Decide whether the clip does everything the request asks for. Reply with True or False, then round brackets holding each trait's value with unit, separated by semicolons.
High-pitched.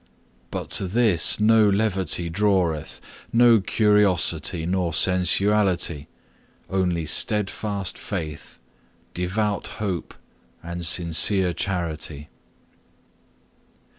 False (95 Hz)